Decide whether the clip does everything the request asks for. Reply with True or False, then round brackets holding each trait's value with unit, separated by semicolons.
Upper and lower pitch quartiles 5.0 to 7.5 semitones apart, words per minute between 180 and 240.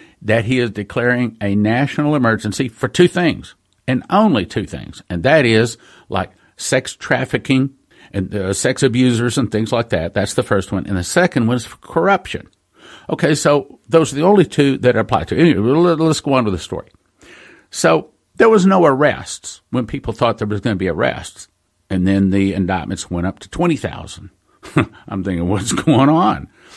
True (5.6 semitones; 190 wpm)